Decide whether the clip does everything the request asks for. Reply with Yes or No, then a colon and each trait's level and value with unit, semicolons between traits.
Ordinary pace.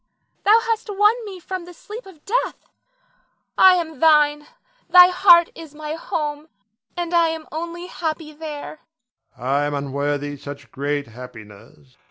Yes: average, 150 wpm